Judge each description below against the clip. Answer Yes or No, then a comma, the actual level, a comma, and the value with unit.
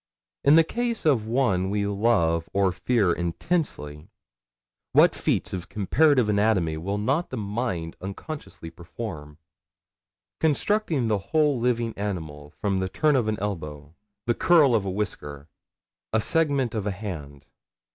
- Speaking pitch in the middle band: No, low, 105 Hz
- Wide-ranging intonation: Yes, wide, 6.7 semitones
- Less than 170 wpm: Yes, average, 140 wpm